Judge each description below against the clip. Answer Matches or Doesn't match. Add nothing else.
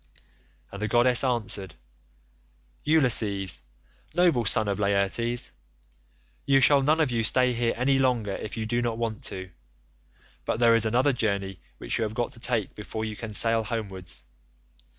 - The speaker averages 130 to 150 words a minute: Doesn't match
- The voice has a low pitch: Matches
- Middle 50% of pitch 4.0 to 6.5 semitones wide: Doesn't match